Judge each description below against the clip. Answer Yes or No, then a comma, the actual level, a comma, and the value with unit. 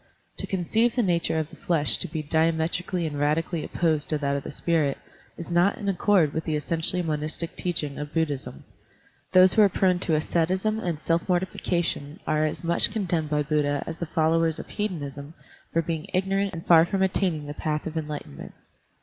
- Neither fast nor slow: Yes, average, 195 wpm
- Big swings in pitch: No, average, 2.9 semitones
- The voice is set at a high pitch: No, medium, 165 Hz